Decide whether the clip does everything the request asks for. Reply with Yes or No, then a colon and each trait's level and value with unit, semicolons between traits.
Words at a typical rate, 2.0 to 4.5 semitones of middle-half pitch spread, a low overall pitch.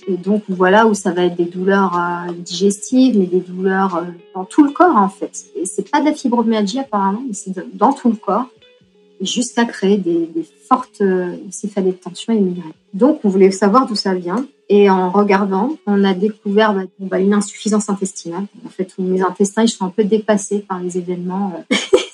No: average, 210 wpm; average, 2.7 semitones; high, 200 Hz